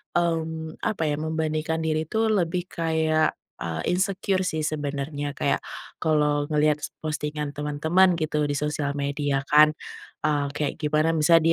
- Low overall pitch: No, medium, 155 Hz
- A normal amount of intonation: No, narrow, 1.6 semitones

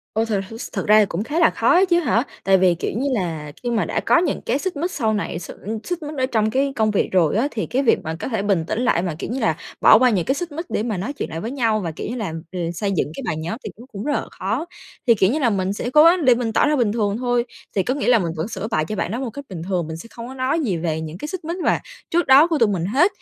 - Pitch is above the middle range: Yes, high, 225 Hz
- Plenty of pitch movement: Yes, wide, 6.2 semitones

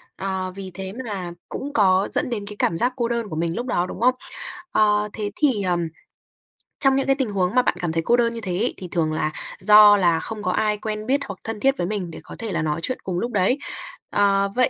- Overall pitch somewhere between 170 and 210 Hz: Yes, high, 205 Hz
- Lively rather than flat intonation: No, average, 4.2 semitones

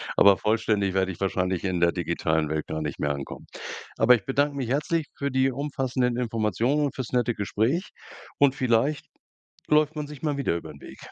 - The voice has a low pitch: Yes, low, 120 Hz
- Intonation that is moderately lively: No, wide, 6.9 semitones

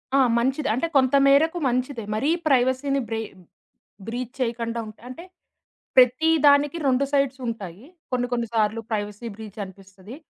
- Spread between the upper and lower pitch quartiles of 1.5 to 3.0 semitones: No, average, 3.6 semitones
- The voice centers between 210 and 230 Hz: No, very high, 250 Hz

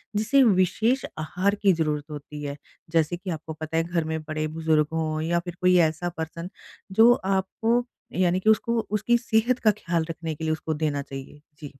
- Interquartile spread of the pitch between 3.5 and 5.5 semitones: Yes, average, 4.3 semitones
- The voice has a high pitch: No, medium, 165 Hz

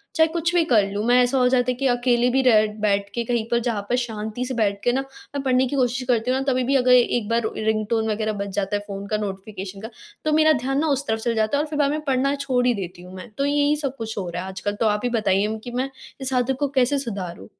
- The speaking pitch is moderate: No, high, 245 Hz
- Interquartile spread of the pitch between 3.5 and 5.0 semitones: Yes, average, 4.0 semitones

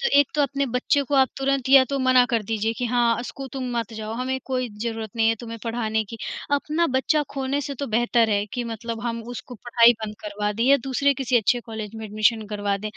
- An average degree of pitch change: Yes, average, 3.1 semitones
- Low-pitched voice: No, high, 240 Hz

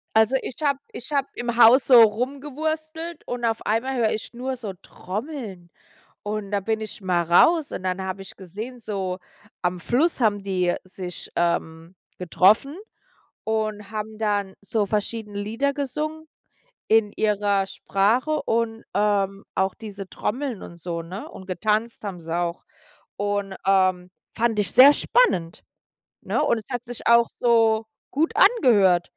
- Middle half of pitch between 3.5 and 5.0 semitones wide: Yes, average, 4.2 semitones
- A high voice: Yes, high, 215 Hz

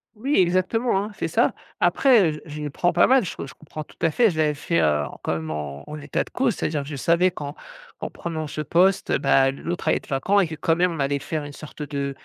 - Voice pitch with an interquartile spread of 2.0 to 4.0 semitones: No, average, 4.4 semitones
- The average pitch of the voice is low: No, medium, 155 Hz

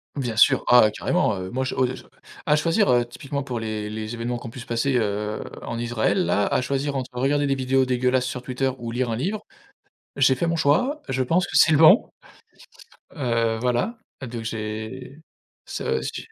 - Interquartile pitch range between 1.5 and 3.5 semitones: Yes, average, 3.1 semitones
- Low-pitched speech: Yes, low, 125 Hz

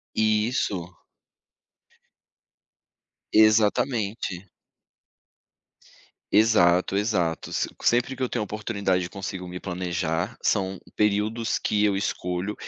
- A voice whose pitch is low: Yes, low, 100 Hz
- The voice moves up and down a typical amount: Yes, average, 3.1 semitones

